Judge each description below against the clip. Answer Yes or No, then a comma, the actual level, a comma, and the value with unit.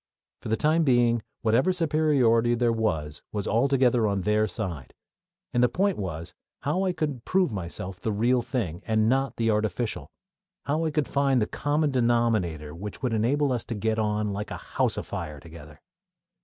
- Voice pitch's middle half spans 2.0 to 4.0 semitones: No, average, 4.8 semitones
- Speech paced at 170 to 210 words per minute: Yes, average, 175 wpm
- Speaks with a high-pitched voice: No, low, 115 Hz